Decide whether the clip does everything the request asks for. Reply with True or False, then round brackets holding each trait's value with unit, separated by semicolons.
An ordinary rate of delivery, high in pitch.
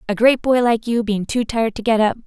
False (290 wpm; 225 Hz)